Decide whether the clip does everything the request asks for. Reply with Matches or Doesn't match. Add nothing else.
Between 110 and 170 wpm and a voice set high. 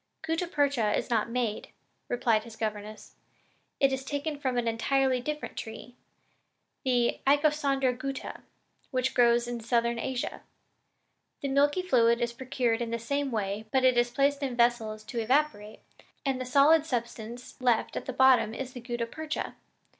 Matches